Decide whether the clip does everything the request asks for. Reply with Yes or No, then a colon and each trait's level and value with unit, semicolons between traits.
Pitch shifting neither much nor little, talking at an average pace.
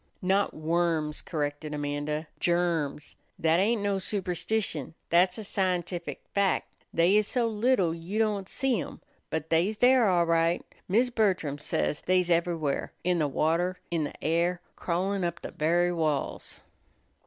Yes: average, 3.4 semitones; average, 145 wpm